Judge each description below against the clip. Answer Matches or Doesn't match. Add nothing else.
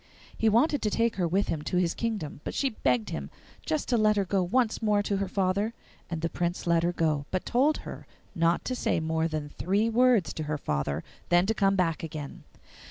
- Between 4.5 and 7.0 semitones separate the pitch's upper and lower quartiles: Matches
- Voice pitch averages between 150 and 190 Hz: Matches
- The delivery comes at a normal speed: Doesn't match